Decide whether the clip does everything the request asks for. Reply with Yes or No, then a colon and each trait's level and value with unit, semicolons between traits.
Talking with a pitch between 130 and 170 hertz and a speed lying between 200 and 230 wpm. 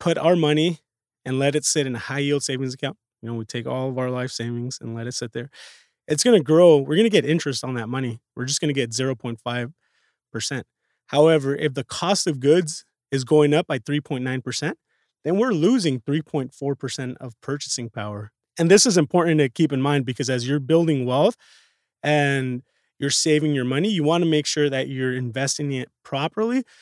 Yes: medium, 140 Hz; fast, 205 wpm